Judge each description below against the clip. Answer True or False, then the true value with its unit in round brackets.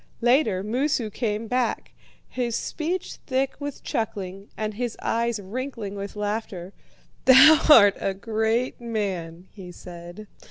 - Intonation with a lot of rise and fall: False (4.0 semitones)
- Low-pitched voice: False (220 Hz)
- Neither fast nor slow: False (125 wpm)